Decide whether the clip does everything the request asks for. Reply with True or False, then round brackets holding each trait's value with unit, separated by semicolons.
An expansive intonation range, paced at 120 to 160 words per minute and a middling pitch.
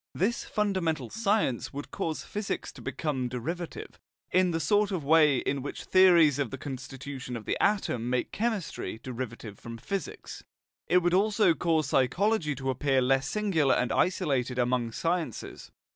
True (6.3 semitones; 155 wpm; 150 Hz)